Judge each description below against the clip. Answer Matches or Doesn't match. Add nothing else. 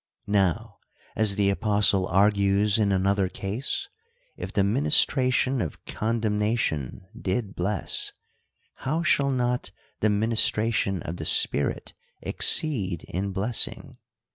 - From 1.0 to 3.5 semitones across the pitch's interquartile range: Matches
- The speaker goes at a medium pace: Doesn't match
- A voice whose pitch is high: Doesn't match